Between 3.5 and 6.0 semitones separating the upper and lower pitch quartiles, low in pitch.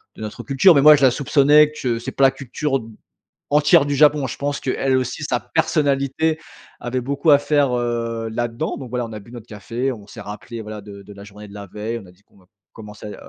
Yes: average, 4.7 semitones; low, 125 Hz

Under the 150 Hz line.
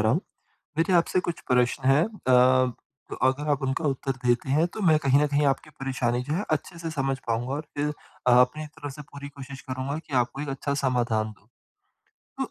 Yes: low, 135 Hz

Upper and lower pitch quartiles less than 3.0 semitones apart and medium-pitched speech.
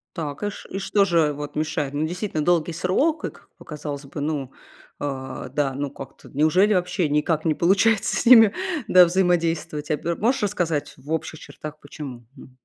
No: average, 3.8 semitones; medium, 160 Hz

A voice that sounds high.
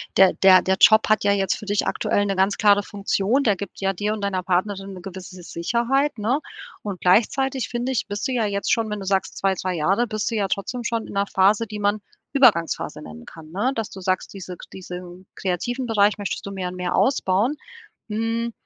Yes: high, 200 Hz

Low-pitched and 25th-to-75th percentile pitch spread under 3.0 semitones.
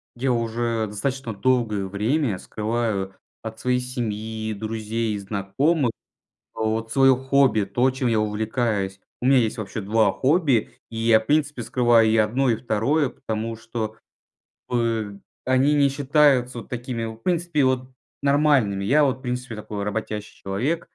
No: low, 115 Hz; average, 3.3 semitones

